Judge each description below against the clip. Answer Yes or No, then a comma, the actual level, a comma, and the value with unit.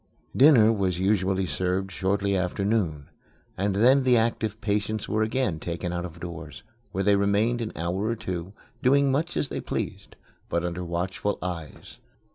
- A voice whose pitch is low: Yes, low, 100 Hz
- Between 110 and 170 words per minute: Yes, average, 165 wpm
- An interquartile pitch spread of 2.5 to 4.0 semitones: Yes, average, 3.7 semitones